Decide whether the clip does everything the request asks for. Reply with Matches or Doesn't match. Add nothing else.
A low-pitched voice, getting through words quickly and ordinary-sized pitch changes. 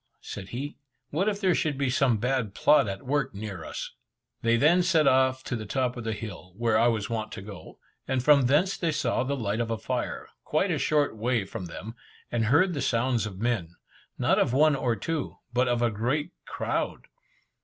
Matches